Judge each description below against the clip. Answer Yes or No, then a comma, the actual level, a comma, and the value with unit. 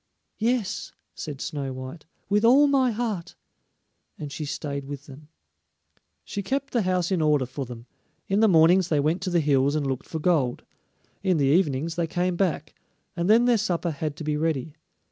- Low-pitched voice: No, medium, 165 Hz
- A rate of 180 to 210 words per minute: Yes, average, 185 wpm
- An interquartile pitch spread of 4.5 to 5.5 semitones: Yes, average, 5.2 semitones